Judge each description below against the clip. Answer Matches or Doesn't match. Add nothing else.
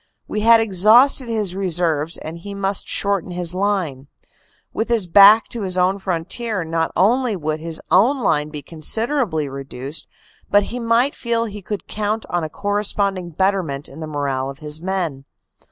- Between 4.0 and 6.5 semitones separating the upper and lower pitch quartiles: Matches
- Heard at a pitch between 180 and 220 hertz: Matches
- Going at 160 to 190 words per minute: Matches